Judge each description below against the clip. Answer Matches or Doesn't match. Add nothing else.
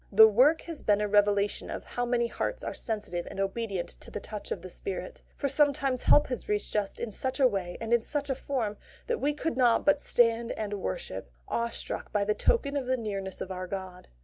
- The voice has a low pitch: Doesn't match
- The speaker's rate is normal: Doesn't match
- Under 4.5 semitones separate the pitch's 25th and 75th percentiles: Doesn't match